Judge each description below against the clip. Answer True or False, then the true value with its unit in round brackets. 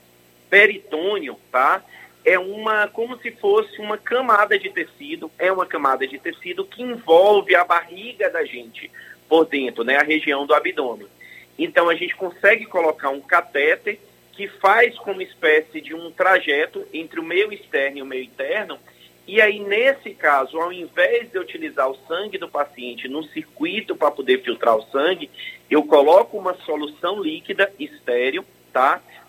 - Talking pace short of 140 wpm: False (160 wpm)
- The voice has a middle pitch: False (200 Hz)